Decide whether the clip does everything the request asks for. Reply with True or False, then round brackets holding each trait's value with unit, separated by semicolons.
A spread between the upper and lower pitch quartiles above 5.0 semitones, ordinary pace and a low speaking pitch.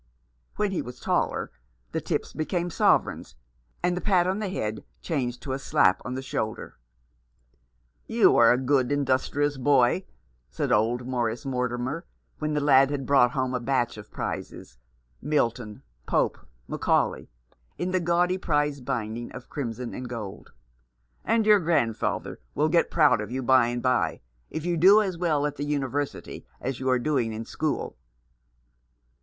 False (4.2 semitones; 165 wpm; 130 Hz)